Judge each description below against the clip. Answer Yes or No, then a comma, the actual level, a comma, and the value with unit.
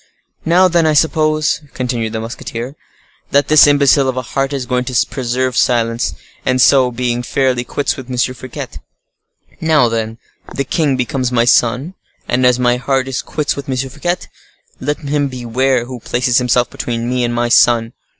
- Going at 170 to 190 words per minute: Yes, average, 175 wpm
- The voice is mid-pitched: No, low, 125 Hz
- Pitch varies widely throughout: No, narrow, 2.5 semitones